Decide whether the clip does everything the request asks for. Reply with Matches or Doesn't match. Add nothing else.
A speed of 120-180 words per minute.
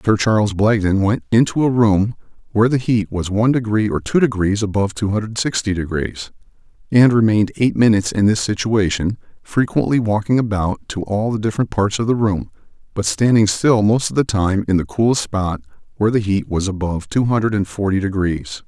Doesn't match